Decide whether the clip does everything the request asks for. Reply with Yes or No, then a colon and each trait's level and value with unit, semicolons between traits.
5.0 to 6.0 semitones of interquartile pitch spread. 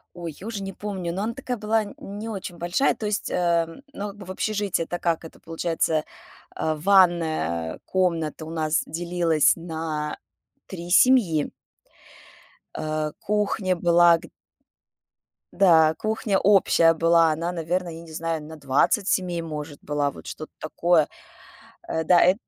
No: average, 3.4 semitones